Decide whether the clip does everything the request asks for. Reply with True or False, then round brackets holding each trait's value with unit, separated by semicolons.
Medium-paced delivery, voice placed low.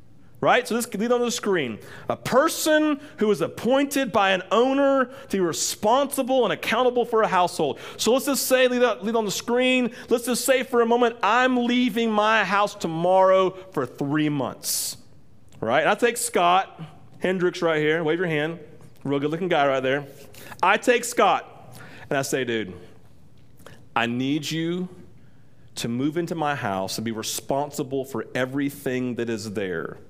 False (170 wpm; 180 Hz)